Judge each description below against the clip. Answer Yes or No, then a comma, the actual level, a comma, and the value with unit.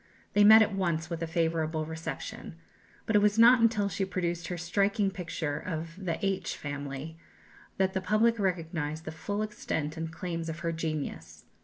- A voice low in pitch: No, medium, 170 Hz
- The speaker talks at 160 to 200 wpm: Yes, average, 175 wpm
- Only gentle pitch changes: No, average, 3.7 semitones